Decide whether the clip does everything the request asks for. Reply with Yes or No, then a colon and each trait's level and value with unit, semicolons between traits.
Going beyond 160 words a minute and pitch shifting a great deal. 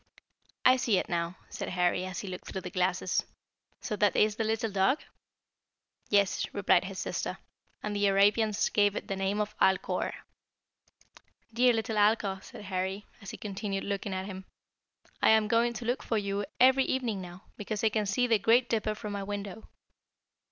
No: average, 180 wpm; narrow, 2.4 semitones